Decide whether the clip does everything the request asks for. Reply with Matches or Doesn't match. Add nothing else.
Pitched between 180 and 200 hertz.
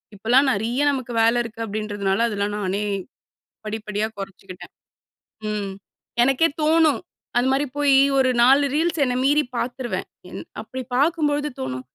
Doesn't match